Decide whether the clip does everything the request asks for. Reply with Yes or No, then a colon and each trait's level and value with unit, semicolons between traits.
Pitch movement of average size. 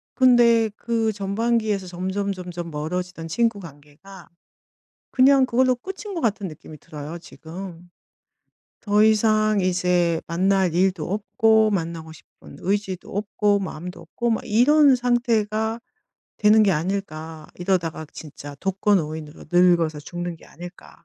Yes: average, 4.5 semitones